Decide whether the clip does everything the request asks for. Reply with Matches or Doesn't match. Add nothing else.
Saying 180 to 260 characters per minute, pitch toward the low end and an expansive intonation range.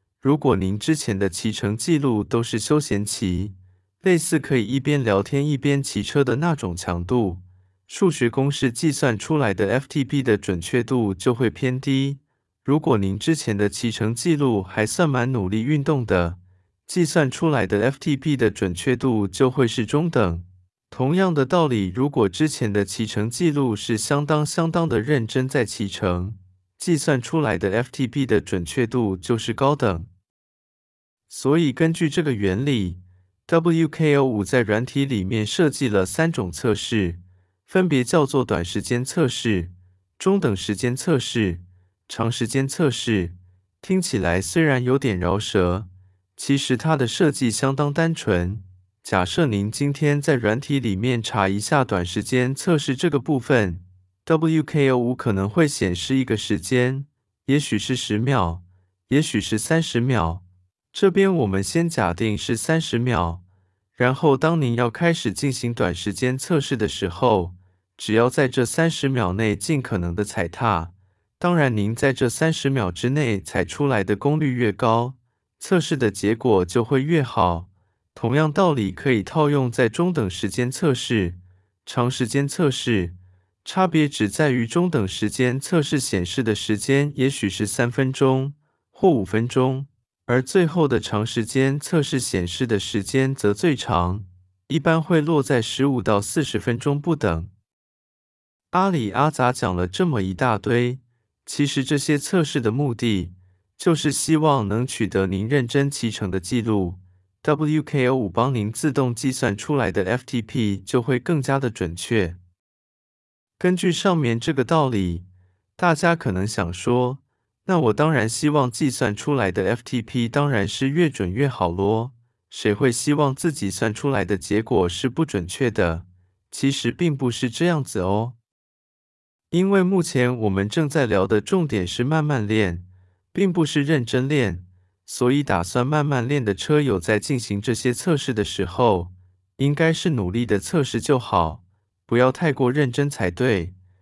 Matches